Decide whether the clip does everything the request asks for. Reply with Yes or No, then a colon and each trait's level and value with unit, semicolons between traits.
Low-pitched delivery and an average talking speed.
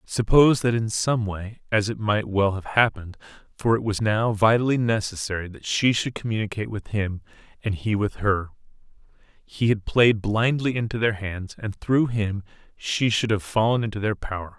Yes: low, 105 Hz; average, 180 wpm